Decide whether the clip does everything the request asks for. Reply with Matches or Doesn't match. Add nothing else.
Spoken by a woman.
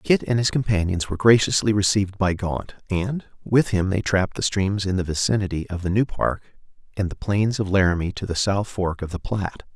Doesn't match